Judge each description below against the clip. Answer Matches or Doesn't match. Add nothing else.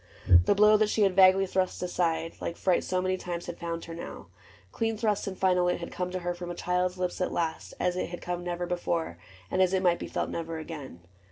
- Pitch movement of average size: Doesn't match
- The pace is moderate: Doesn't match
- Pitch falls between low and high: Matches